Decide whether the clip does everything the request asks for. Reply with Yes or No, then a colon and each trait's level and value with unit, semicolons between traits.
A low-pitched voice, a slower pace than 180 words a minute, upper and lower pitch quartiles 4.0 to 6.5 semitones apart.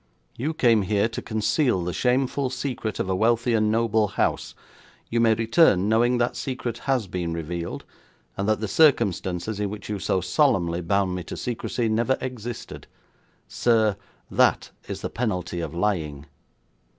Yes: low, 110 Hz; average, 160 wpm; average, 4.4 semitones